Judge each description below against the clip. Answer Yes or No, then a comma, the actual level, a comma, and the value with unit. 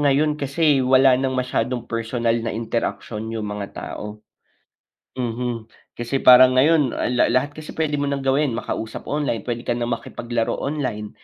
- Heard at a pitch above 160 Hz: No, low, 125 Hz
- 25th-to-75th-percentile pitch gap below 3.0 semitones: No, average, 3.3 semitones